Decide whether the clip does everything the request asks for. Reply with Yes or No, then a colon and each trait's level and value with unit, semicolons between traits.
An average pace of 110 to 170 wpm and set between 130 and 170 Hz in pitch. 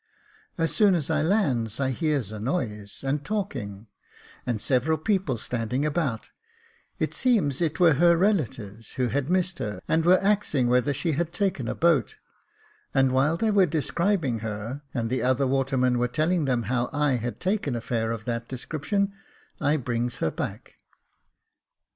Yes: average, 165 wpm; low, 135 Hz